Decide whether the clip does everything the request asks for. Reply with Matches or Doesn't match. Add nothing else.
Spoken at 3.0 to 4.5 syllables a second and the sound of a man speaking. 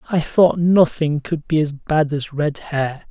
Matches